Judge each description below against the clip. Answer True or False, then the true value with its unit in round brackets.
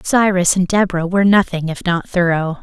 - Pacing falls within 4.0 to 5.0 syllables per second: False (5.6 syllables/s)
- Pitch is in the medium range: True (180 Hz)